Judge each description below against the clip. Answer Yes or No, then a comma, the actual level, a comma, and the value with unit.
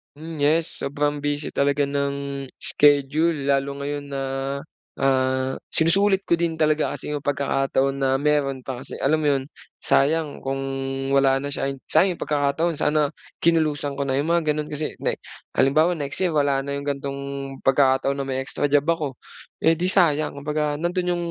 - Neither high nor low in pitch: Yes, medium, 145 Hz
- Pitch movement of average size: No, narrow, 2.2 semitones